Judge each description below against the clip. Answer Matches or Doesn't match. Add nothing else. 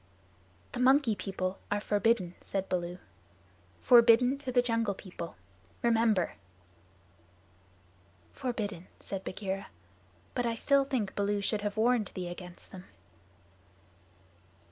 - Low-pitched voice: Doesn't match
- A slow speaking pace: Matches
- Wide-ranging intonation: Doesn't match